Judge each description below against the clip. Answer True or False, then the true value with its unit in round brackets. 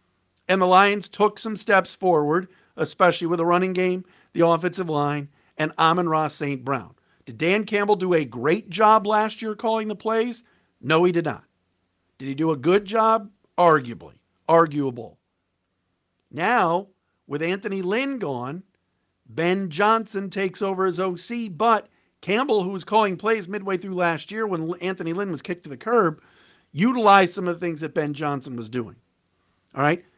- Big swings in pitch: True (5.7 semitones)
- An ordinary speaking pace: True (170 wpm)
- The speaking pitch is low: False (175 Hz)